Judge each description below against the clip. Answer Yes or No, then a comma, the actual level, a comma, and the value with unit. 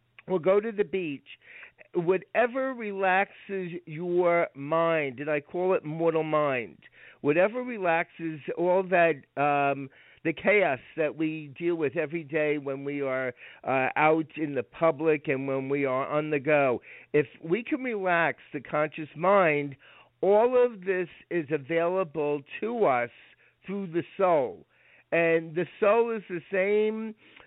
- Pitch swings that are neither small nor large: Yes, average, 4.2 semitones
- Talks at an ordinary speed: Yes, average, 145 wpm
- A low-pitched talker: No, medium, 165 Hz